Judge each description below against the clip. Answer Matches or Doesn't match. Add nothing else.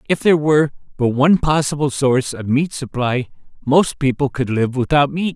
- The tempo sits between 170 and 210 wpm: Matches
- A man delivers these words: Matches